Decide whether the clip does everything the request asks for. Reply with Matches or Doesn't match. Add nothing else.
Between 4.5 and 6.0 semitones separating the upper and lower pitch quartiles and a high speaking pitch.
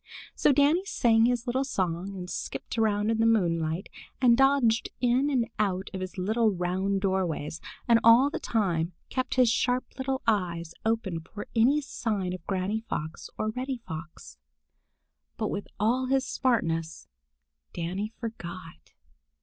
Matches